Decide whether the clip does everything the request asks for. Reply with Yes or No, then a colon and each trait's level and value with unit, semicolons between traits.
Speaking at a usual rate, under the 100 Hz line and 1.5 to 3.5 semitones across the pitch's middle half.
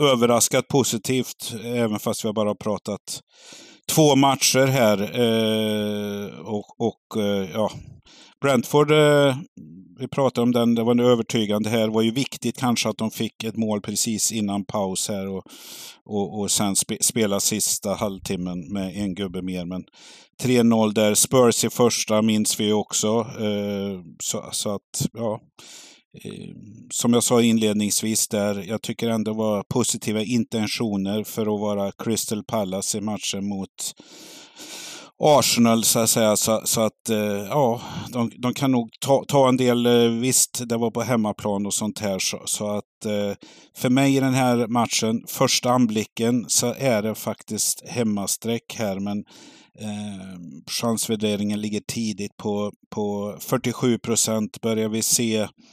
No: average, 155 wpm; low, 110 Hz; narrow, 2.5 semitones